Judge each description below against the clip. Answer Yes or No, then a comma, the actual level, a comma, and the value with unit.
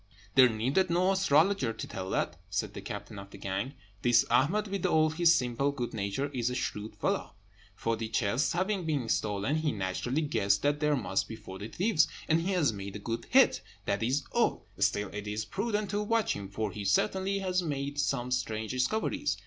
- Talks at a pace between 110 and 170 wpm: No, average, 195 wpm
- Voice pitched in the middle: No, low, 130 Hz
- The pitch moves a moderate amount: No, wide, 7.7 semitones